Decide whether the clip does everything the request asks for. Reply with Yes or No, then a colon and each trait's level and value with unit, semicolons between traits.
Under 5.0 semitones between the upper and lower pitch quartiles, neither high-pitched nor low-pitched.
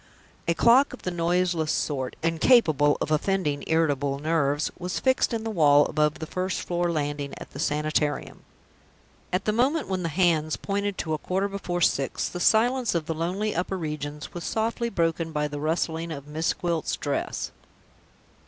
Yes: average, 3.9 semitones; medium, 165 Hz